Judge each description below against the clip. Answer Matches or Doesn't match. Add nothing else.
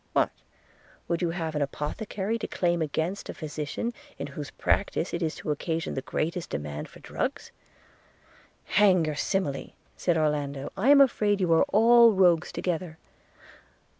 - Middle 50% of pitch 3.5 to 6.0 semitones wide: Matches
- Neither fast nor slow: Matches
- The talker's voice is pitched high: Doesn't match